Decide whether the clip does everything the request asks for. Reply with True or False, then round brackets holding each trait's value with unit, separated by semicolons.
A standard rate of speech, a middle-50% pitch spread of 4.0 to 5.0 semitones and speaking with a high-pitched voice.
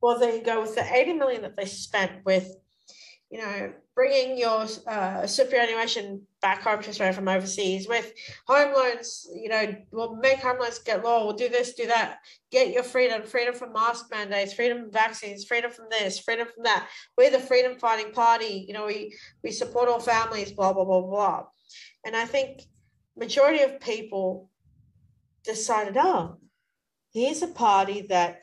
False (175 wpm; 3.4 semitones; 225 Hz)